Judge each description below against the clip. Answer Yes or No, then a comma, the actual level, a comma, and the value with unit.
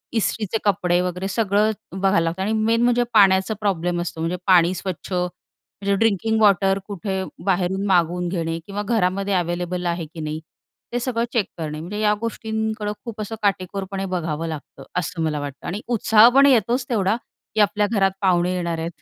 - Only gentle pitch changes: No, average, 3.4 semitones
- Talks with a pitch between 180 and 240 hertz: Yes, high, 190 Hz